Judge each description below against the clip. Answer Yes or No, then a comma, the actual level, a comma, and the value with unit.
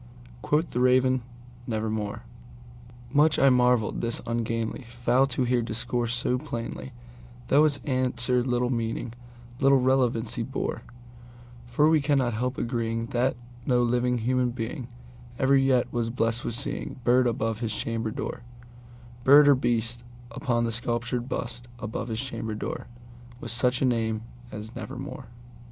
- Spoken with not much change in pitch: Yes, narrow, 1.4 semitones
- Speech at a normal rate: No, slow, 125 wpm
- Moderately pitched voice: No, low, 120 Hz